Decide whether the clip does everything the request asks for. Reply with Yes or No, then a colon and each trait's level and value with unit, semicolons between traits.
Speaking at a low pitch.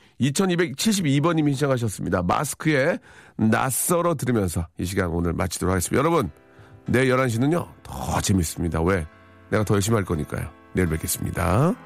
Yes: low, 105 Hz